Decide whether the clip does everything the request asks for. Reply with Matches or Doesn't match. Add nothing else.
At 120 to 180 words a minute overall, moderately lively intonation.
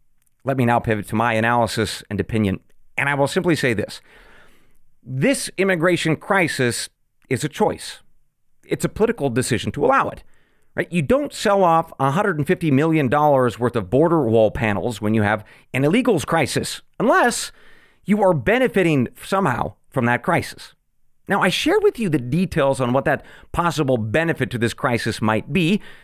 Doesn't match